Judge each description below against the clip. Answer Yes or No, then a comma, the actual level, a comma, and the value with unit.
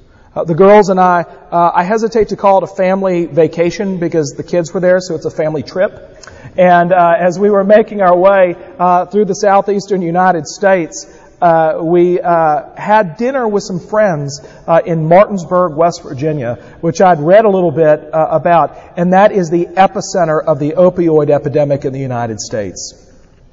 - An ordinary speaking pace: Yes, average, 185 wpm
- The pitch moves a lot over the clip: No, average, 3.2 semitones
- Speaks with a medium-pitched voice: Yes, medium, 175 Hz